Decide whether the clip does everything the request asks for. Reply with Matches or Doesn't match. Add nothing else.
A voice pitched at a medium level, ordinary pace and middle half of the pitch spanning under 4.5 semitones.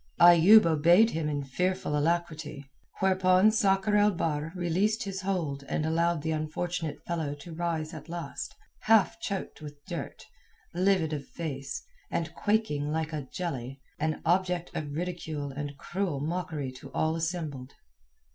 Matches